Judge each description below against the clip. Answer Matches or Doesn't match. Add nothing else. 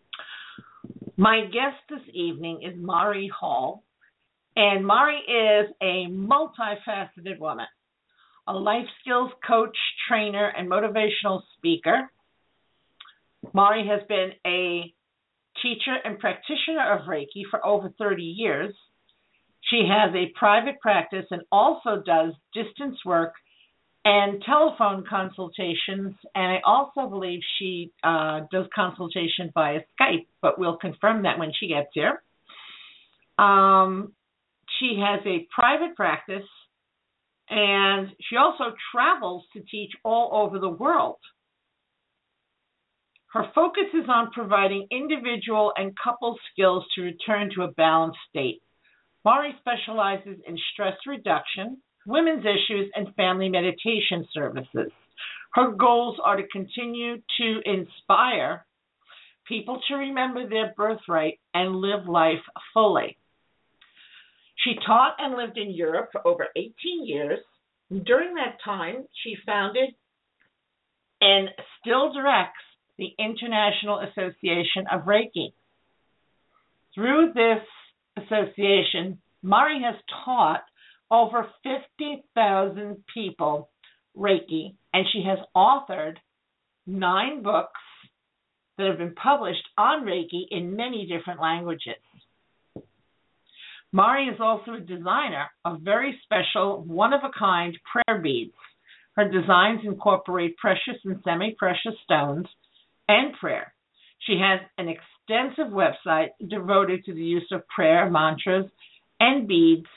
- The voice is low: Doesn't match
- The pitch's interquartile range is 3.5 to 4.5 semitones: Matches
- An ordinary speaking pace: Doesn't match